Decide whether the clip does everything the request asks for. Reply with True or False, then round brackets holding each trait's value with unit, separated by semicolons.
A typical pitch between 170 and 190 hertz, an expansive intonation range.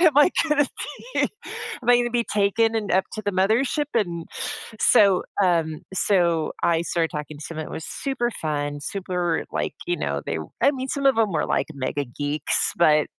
True (185 Hz; 7.3 semitones)